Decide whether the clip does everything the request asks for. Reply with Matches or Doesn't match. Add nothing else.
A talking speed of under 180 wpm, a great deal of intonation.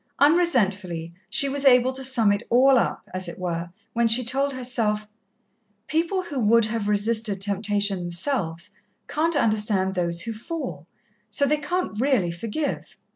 Matches